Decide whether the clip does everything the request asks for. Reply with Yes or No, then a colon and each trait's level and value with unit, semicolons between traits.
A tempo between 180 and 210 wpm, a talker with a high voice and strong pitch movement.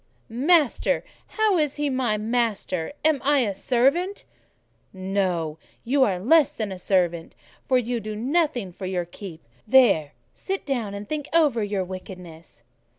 No: average, 150 wpm; high, 215 Hz; wide, 7.0 semitones